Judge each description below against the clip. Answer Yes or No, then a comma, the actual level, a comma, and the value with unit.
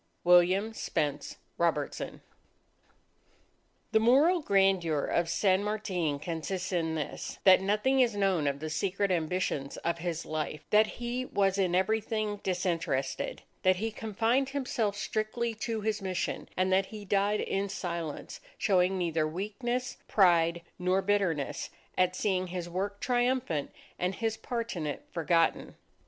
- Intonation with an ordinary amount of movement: Yes, average, 3.9 semitones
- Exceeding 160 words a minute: No, average, 140 wpm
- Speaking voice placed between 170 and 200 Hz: Yes, high, 190 Hz